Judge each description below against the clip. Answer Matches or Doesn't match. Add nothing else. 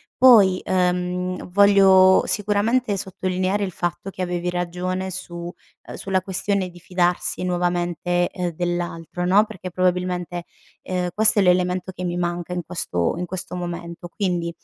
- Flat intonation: Matches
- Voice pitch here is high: Doesn't match